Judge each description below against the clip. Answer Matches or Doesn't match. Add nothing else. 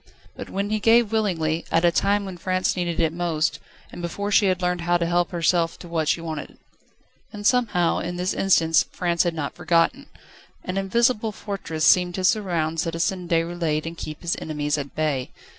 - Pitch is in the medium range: Matches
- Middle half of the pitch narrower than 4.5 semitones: Matches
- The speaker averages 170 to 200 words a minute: Matches